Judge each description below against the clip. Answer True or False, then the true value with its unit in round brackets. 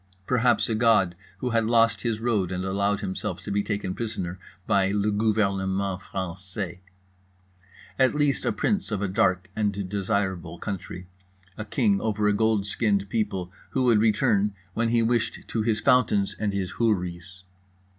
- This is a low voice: True (105 Hz)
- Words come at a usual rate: True (160 wpm)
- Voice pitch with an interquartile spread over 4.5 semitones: False (3.0 semitones)